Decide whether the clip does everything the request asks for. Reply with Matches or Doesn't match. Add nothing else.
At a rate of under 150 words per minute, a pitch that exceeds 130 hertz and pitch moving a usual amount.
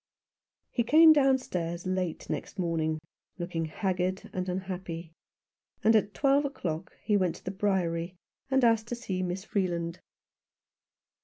Matches